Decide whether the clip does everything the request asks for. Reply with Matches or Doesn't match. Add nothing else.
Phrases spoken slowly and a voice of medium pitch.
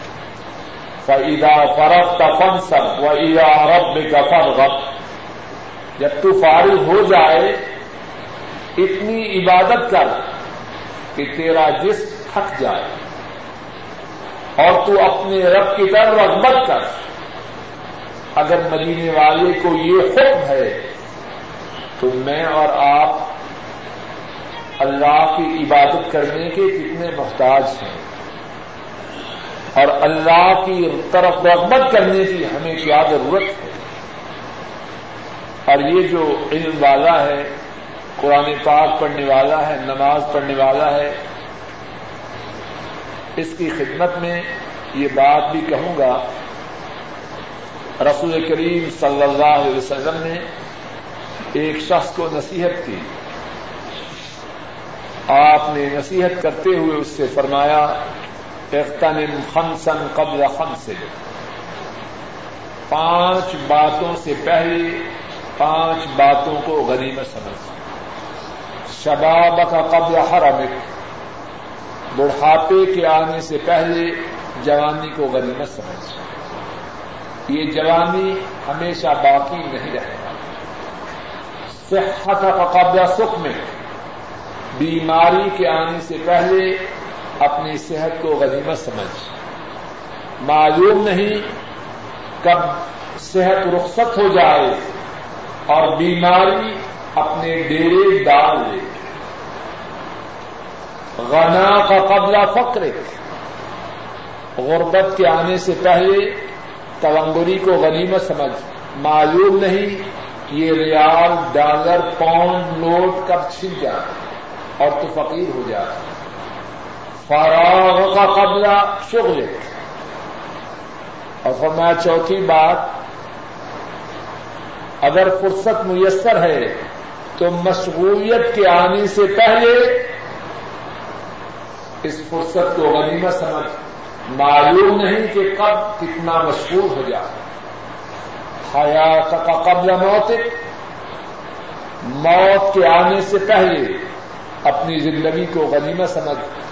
Matches